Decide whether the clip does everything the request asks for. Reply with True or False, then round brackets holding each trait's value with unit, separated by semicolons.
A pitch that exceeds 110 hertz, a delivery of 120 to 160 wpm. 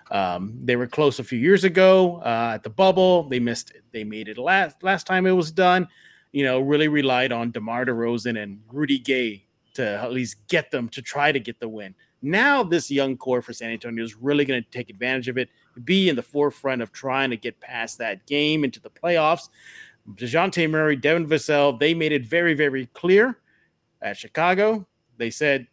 False (135 Hz; 205 wpm)